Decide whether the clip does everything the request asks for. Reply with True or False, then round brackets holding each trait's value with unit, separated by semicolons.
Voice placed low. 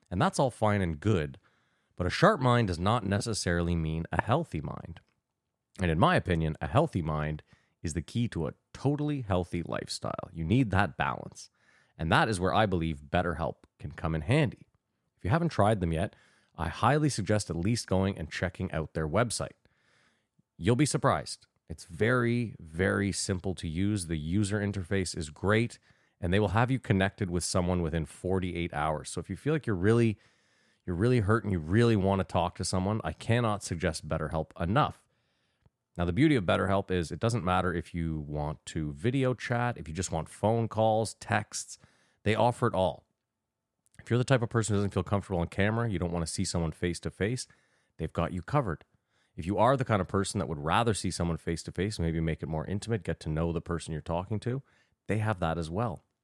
True (95 Hz)